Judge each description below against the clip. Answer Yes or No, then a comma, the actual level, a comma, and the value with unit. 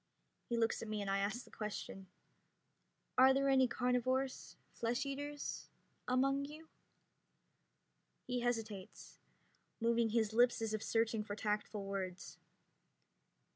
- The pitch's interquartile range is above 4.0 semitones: No, average, 3.5 semitones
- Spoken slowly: Yes, slow, 125 wpm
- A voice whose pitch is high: Yes, high, 230 Hz